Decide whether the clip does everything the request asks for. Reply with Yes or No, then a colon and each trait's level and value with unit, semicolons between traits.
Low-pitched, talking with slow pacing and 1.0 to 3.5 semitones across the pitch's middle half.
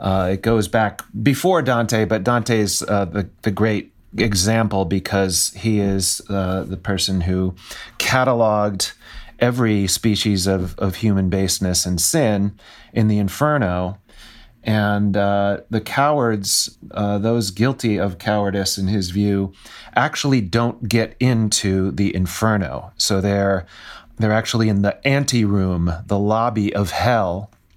Yes: low, 105 Hz; slow, 130 wpm; narrow, 2.6 semitones